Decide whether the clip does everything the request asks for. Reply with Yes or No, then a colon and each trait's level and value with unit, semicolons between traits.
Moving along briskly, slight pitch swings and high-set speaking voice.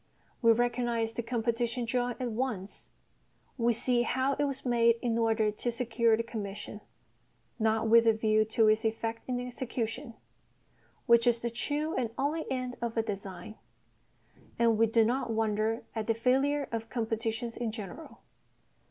No: average, 160 wpm; narrow, 1.7 semitones; high, 230 Hz